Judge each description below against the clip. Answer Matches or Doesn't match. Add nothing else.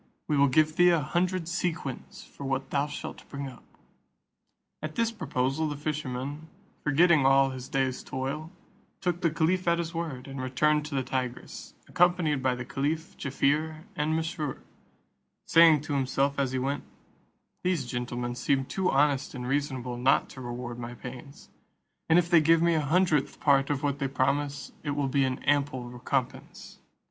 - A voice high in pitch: Doesn't match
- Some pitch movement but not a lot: Matches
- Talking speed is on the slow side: Doesn't match